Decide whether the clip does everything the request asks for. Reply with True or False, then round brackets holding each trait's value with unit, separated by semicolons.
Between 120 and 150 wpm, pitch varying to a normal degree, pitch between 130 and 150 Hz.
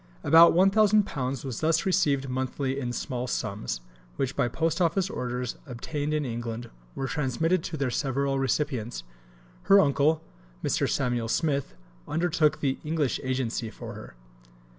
True (140 wpm; 4.3 semitones; 140 Hz)